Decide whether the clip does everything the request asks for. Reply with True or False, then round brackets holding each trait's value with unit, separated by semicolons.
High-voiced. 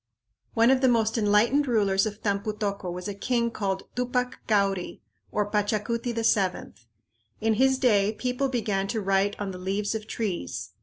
True (210 Hz)